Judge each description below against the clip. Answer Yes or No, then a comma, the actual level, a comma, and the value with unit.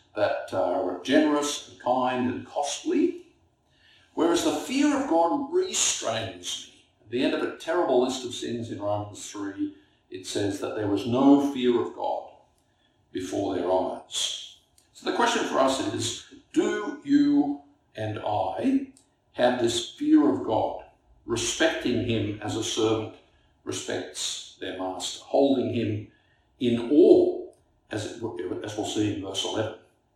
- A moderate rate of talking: Yes, average, 145 wpm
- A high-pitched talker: No, medium, 145 Hz